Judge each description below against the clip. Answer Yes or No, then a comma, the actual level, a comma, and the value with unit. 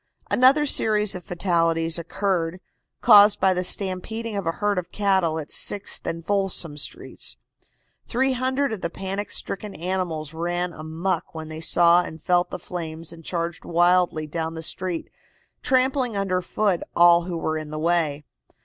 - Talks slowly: No, average, 160 wpm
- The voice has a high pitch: No, medium, 175 Hz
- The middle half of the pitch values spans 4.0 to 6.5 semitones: No, average, 3.4 semitones